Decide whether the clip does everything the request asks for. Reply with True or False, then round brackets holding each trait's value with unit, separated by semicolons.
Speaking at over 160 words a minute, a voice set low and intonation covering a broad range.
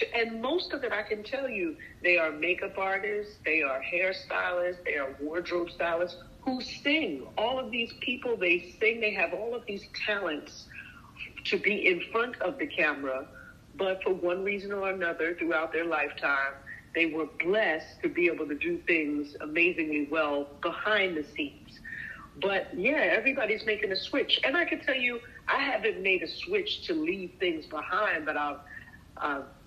False (170 wpm; 190 Hz; 7.0 semitones)